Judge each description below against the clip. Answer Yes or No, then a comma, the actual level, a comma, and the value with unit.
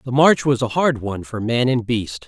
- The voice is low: Yes, low, 125 Hz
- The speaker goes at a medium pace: No, fast, 265 wpm